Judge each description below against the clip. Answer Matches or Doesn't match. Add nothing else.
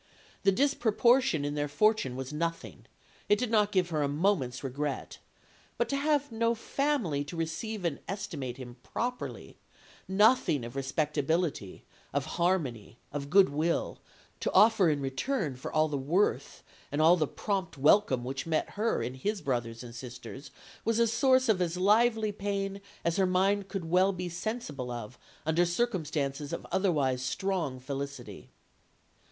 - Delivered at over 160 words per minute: Doesn't match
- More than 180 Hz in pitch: Doesn't match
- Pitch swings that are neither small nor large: Doesn't match